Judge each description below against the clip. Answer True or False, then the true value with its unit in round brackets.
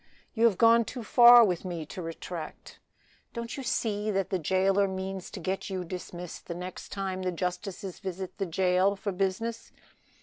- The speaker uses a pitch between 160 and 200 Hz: True (190 Hz)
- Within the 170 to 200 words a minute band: True (175 wpm)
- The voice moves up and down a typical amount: False (2.3 semitones)